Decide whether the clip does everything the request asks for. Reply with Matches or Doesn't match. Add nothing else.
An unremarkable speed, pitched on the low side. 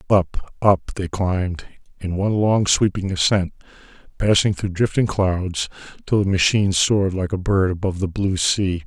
Matches